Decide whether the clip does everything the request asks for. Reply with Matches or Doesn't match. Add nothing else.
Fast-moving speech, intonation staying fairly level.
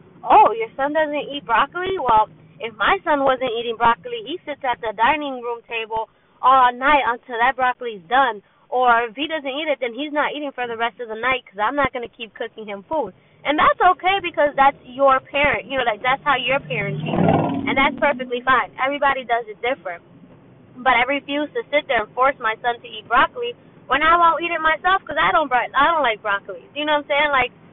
Doesn't match